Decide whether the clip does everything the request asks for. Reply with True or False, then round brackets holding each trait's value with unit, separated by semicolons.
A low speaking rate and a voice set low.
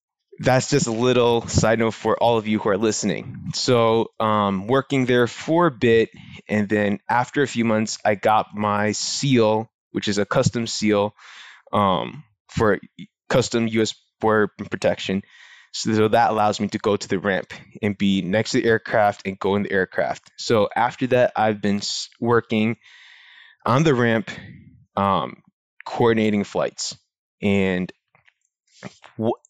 False (155 wpm; 110 Hz)